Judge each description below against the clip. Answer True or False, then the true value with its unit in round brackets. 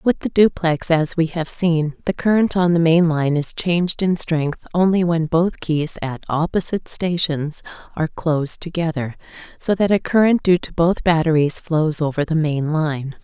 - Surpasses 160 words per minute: True (180 wpm)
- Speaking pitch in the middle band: True (165 Hz)